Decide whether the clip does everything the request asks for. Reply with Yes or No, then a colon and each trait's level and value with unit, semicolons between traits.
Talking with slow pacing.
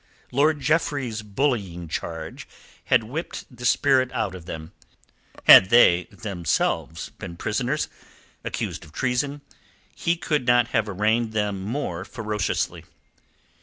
Yes: slow, 120 wpm